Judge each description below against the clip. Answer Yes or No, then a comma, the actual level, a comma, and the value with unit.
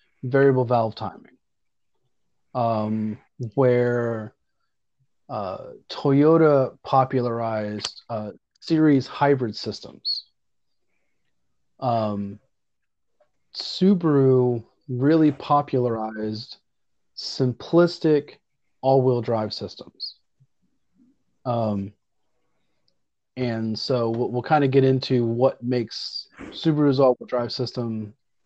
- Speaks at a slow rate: Yes, slow, 80 wpm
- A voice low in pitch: Yes, low, 125 Hz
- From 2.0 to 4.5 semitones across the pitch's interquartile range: Yes, average, 3.4 semitones